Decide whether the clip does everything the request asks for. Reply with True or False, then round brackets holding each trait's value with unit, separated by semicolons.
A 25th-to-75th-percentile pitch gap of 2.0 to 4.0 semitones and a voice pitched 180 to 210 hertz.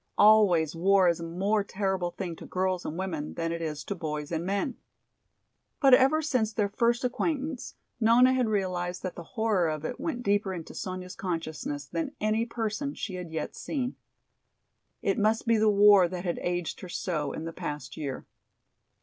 False (4.5 semitones; 190 Hz)